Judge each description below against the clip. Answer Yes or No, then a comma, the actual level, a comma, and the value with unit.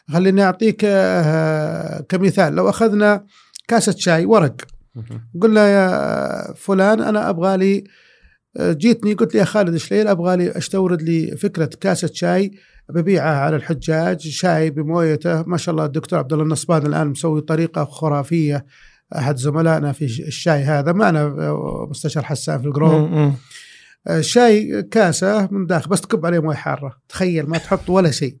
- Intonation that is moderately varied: Yes, average, 4.0 semitones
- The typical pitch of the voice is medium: Yes, medium, 165 Hz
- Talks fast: Yes, fast, 140 wpm